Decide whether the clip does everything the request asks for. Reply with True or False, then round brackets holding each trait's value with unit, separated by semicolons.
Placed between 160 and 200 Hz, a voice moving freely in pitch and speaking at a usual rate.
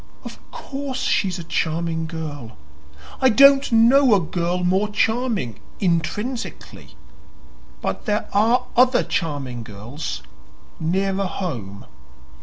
False (185 Hz; 6.7 semitones; 105 wpm)